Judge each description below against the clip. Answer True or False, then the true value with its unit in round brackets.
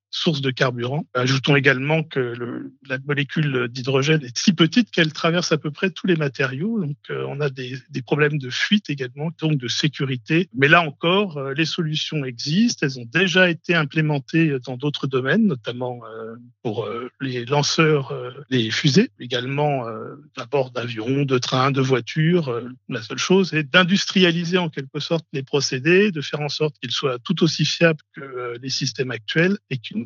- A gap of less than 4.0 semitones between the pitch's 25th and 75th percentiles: False (4.3 semitones)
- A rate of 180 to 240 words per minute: True (185 wpm)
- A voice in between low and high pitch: True (145 Hz)